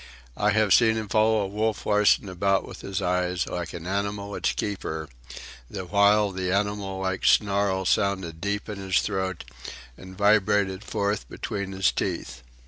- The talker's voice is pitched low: Yes, low, 100 Hz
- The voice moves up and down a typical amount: No, narrow, 1.7 semitones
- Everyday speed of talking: Yes, average, 155 wpm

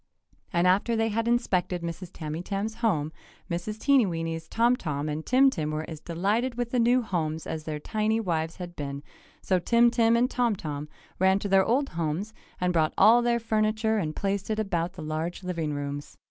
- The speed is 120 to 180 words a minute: No, average, 190 wpm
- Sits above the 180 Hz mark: Yes, high, 190 Hz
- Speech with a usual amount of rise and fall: No, wide, 5.8 semitones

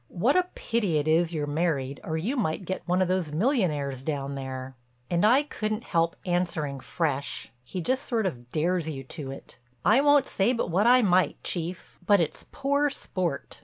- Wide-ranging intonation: Yes, wide, 6.5 semitones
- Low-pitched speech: No, medium, 175 Hz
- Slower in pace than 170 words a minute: No, average, 185 wpm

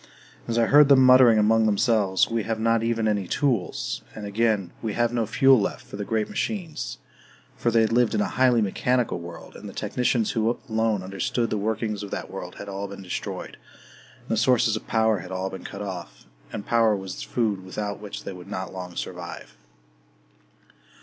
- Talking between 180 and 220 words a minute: Yes, average, 200 wpm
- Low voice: Yes, low, 110 Hz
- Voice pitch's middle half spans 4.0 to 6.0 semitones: No, average, 2.9 semitones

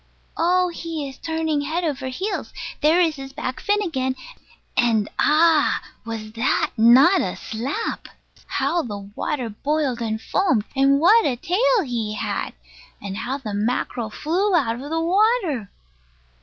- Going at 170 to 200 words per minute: No, average, 150 wpm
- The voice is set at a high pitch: Yes, very high, 280 Hz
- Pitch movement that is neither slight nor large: No, wide, 6.4 semitones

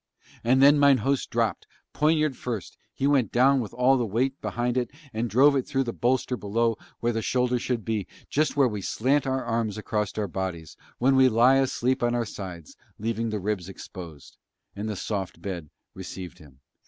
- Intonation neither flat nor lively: Yes, average, 4.3 semitones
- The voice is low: Yes, low, 120 Hz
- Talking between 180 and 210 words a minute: Yes, average, 190 wpm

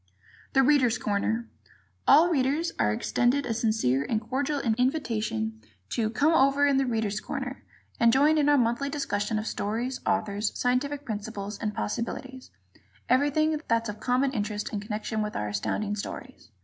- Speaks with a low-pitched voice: No, high, 235 Hz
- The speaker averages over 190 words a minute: No, average, 155 wpm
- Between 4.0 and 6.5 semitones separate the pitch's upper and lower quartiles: Yes, average, 4.6 semitones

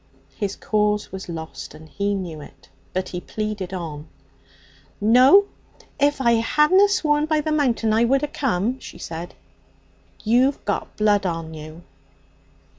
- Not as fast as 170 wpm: Yes, average, 140 wpm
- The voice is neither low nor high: No, high, 210 Hz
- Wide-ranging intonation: Yes, wide, 7.3 semitones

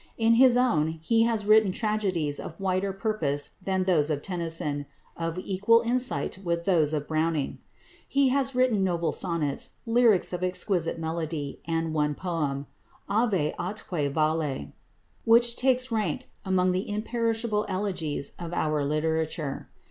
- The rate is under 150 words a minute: Yes, average, 140 wpm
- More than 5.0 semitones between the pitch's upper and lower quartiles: Yes, wide, 5.5 semitones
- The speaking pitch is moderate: Yes, medium, 180 Hz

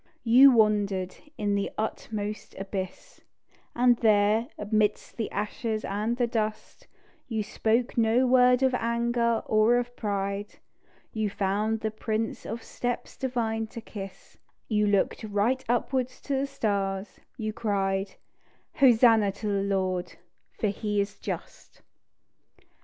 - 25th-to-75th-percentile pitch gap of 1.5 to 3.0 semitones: Yes, average, 2.7 semitones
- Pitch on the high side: Yes, high, 220 Hz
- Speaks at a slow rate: Yes, slow, 130 wpm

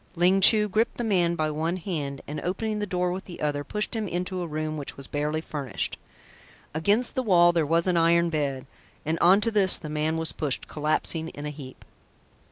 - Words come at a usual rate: No, fast, 210 wpm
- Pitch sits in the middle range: Yes, medium, 170 Hz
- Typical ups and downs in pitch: Yes, average, 3.7 semitones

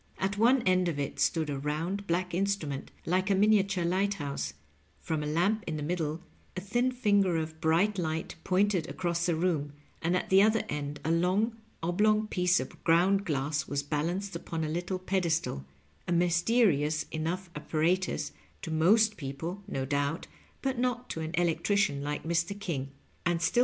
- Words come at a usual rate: Yes, average, 175 wpm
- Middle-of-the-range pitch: Yes, medium, 175 Hz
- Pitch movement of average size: Yes, average, 4.0 semitones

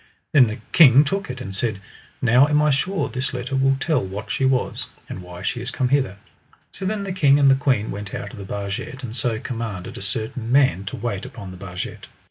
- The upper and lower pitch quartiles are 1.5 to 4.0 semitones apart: No, average, 5.2 semitones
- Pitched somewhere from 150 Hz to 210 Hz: No, low, 125 Hz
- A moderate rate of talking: No, fast, 230 wpm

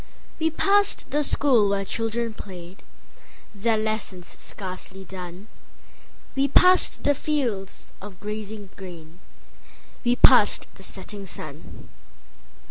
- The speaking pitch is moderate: No, high, 210 Hz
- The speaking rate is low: Yes, slow, 95 wpm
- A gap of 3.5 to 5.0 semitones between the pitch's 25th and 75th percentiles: Yes, average, 4.3 semitones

